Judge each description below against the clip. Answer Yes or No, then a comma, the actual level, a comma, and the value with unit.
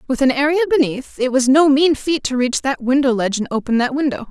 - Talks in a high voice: Yes, very high, 265 Hz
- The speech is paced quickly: Yes, fast, 250 wpm